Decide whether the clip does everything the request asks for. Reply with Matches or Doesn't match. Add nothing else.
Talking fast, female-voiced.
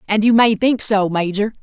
Matches